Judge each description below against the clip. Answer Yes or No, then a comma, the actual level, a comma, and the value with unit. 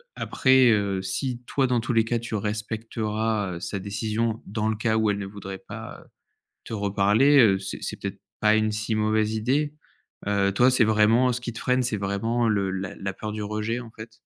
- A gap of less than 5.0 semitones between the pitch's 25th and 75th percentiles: Yes, narrow, 2.4 semitones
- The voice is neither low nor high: No, low, 110 Hz